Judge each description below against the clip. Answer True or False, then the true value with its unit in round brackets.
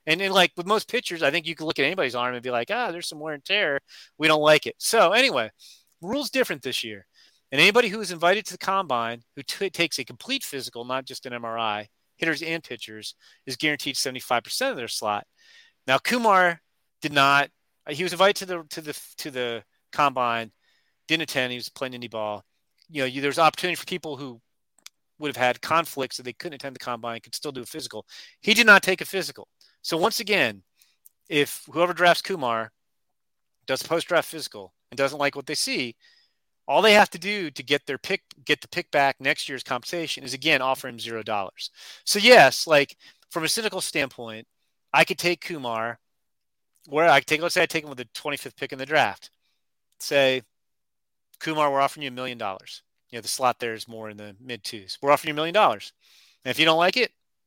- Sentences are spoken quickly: True (215 wpm)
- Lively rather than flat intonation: True (6.1 semitones)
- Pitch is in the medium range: True (145 Hz)